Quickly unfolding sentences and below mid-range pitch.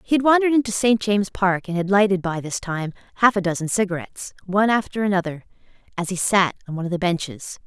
No: fast, 220 wpm; high, 195 Hz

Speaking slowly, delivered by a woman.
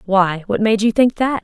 No: fast, 250 wpm; female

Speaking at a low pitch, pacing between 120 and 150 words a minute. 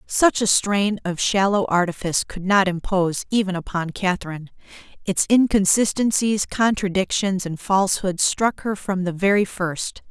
No: high, 190 Hz; slow, 135 wpm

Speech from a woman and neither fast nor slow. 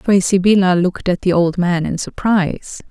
Yes: female; average, 185 wpm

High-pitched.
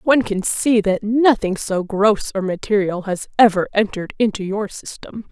Yes: high, 205 Hz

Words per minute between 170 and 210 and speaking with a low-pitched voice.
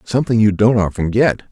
Yes: average, 200 wpm; low, 110 Hz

